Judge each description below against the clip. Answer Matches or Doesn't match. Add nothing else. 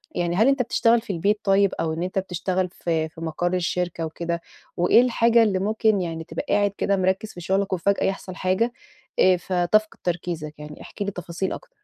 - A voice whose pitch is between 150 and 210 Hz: Matches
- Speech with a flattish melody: Doesn't match